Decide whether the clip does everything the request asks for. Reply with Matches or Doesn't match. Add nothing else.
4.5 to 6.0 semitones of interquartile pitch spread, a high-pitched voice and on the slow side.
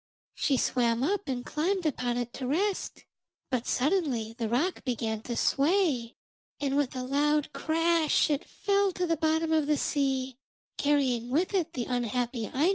Doesn't match